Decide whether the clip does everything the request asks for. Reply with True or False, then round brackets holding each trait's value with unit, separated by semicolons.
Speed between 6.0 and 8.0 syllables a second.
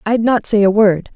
False (4.9 syllables/s)